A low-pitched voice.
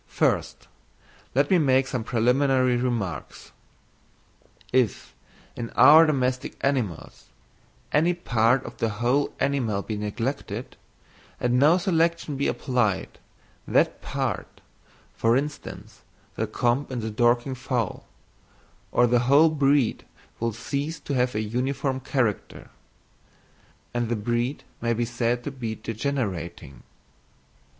Yes: low, 125 Hz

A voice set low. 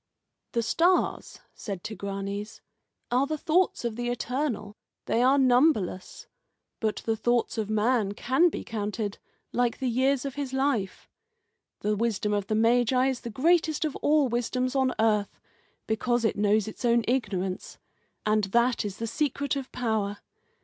No: high, 235 Hz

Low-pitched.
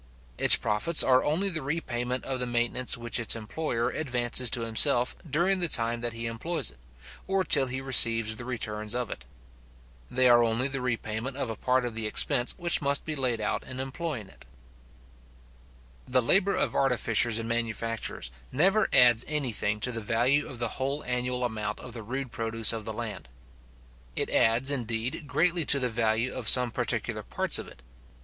Yes: low, 125 Hz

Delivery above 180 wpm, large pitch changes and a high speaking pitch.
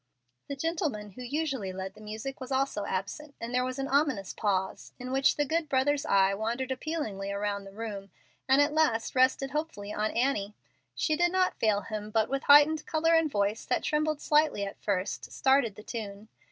Yes: average, 195 wpm; wide, 6.0 semitones; very high, 255 Hz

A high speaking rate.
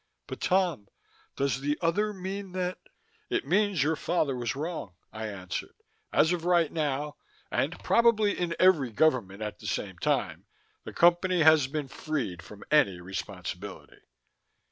No: average, 150 wpm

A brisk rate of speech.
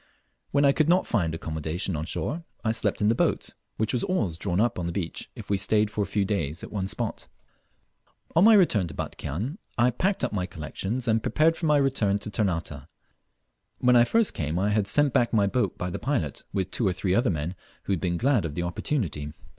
Yes: fast, 225 wpm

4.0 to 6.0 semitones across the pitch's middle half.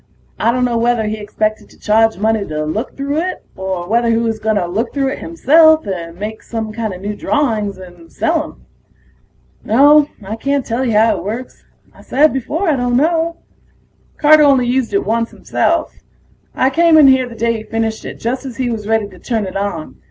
Yes: average, 4.4 semitones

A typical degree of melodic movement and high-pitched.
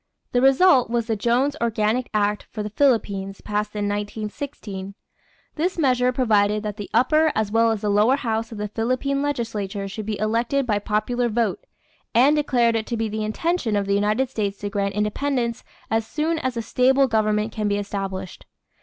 Yes: average, 3.4 semitones; high, 220 Hz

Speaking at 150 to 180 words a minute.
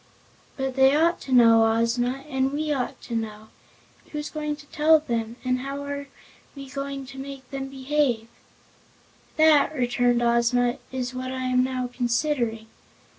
Yes: average, 155 wpm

